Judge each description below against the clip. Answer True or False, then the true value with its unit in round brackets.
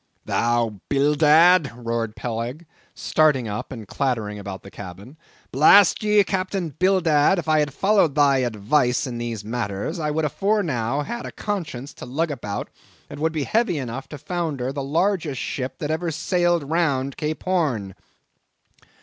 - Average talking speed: True (160 wpm)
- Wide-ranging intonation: True (5.8 semitones)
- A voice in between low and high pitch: True (145 Hz)